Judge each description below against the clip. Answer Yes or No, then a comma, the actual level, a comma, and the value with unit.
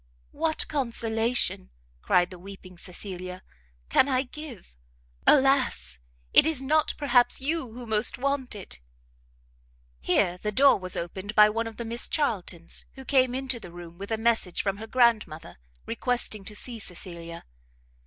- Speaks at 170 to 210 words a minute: No, average, 155 wpm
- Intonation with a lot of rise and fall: Yes, wide, 6.1 semitones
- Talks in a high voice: Yes, high, 220 Hz